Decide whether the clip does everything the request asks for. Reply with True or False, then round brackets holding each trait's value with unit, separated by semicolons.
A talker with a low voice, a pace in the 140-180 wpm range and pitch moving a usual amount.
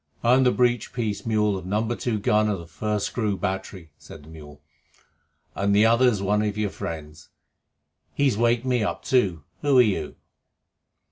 True (105 Hz; 175 wpm; 4.0 semitones)